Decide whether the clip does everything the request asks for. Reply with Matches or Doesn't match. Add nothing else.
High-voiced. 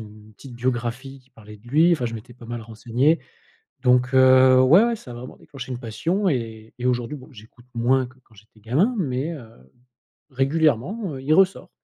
Doesn't match